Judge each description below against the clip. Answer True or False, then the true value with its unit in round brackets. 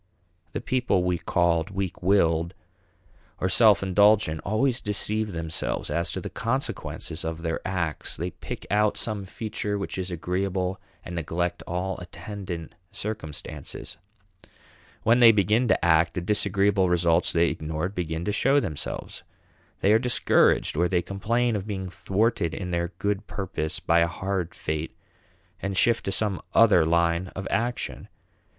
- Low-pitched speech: True (95 Hz)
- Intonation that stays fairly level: False (3.6 semitones)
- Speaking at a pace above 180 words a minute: False (145 wpm)